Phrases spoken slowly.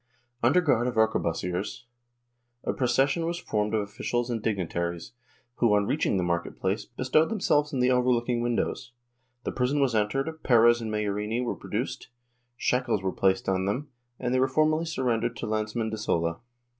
No: average, 175 wpm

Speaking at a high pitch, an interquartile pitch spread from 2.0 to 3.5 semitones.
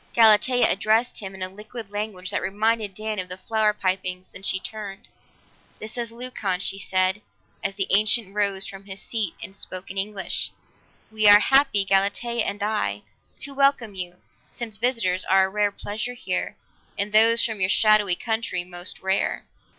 Yes: high, 205 Hz; narrow, 2.5 semitones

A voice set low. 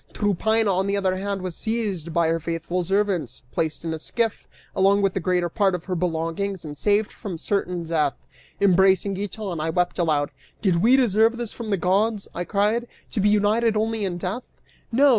No: high, 195 Hz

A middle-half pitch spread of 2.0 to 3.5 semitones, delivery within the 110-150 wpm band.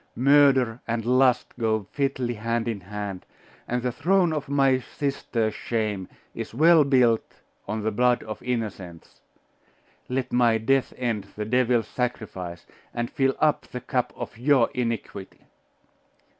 Yes: average, 3.2 semitones; average, 140 wpm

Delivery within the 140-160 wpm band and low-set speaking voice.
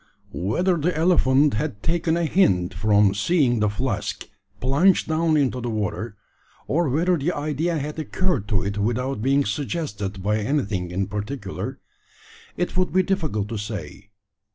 Yes: average, 155 wpm; low, 130 Hz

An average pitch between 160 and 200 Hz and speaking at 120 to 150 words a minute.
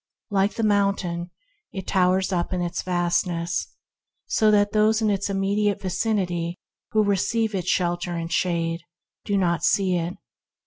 Yes: medium, 185 Hz; average, 145 wpm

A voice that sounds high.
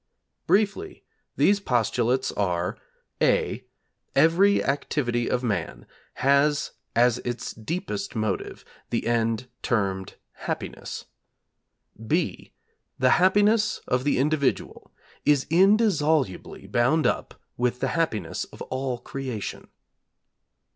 No: low, 130 Hz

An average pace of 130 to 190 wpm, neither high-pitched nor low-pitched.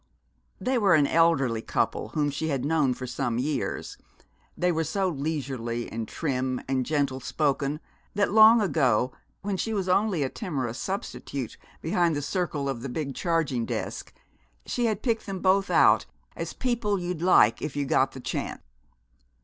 Yes: average, 165 wpm; medium, 150 Hz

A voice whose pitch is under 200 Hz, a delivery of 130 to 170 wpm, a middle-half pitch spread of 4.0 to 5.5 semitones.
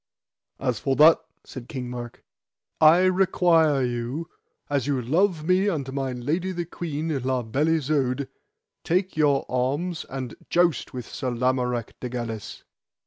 Yes: medium, 140 Hz; average, 140 wpm; average, 4.7 semitones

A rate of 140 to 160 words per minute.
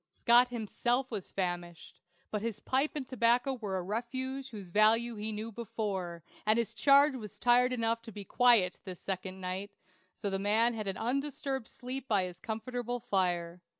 No: average, 175 wpm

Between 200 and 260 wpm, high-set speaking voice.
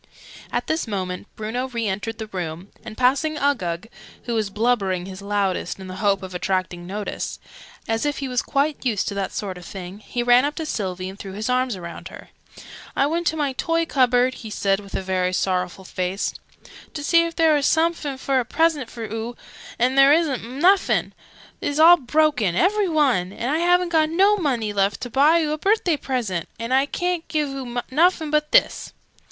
Yes: fast, 205 wpm; high, 245 Hz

